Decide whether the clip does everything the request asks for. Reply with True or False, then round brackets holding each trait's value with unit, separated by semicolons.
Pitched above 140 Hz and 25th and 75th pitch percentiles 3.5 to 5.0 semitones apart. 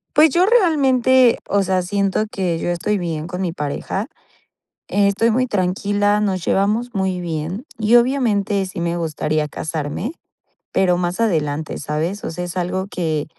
True (190 Hz; 4.0 semitones)